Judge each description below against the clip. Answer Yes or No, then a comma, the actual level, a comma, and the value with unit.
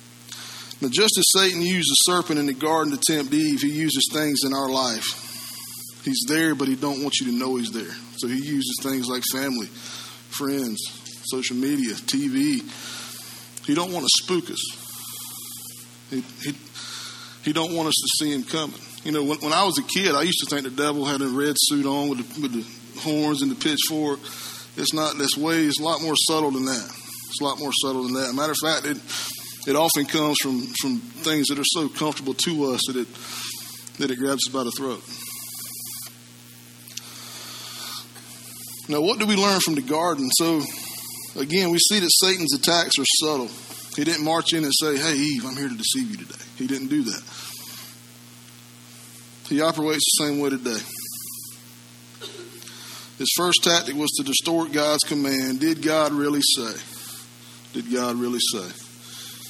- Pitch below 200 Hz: Yes, medium, 140 Hz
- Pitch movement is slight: No, average, 4.8 semitones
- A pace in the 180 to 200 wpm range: Yes, average, 185 wpm